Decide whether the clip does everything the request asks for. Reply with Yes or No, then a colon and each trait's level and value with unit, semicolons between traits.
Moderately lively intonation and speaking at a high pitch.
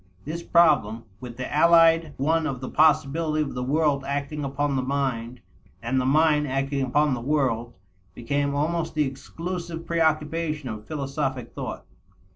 No: average, 3.0 semitones; medium, 145 Hz